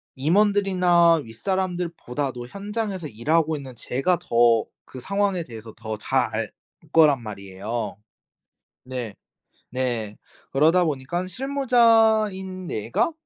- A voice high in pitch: No, medium, 160 Hz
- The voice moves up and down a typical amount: No, wide, 7.9 semitones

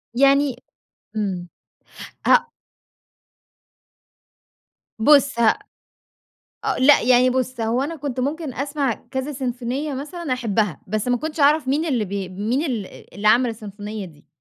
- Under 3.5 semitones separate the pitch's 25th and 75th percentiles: No, average, 4.3 semitones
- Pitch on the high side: Yes, very high, 255 Hz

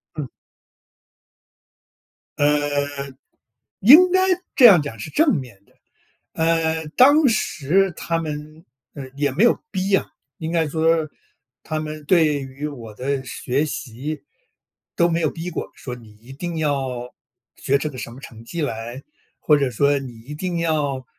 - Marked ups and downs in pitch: No, average, 3.7 semitones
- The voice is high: No, medium, 150 Hz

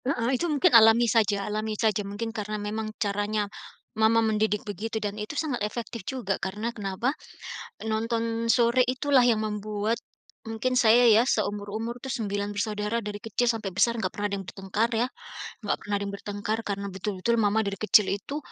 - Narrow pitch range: Yes, narrow, 2.2 semitones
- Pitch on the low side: No, high, 215 Hz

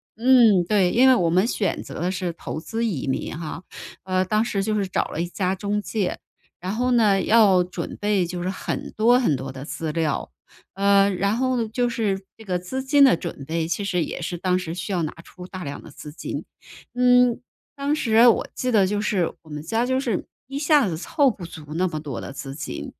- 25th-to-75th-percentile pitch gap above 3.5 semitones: Yes, average, 5.1 semitones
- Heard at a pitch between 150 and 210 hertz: Yes, high, 195 Hz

